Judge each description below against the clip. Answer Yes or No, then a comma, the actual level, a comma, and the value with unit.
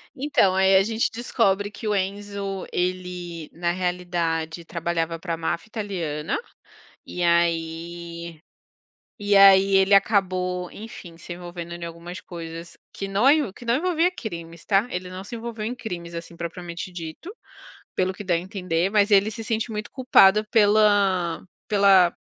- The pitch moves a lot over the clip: No, average, 3.2 semitones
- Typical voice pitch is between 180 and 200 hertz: Yes, medium, 185 Hz